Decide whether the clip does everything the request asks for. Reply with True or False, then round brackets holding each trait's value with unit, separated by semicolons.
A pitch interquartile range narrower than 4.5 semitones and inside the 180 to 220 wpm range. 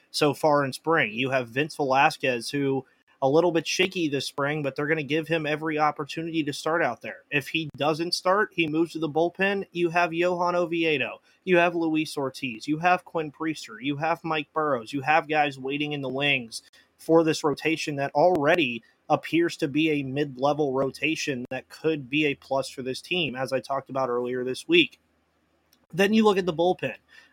True (3.2 semitones; 200 wpm)